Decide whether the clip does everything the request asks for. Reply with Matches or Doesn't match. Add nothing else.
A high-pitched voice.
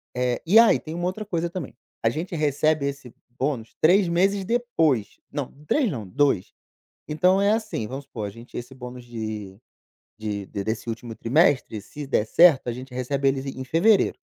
Doesn't match